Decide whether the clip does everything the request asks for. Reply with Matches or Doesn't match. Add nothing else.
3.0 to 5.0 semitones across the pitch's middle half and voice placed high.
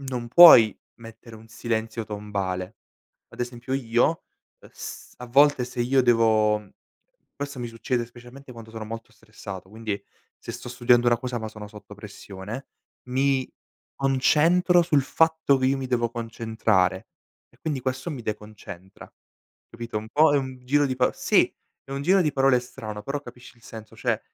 Doesn't match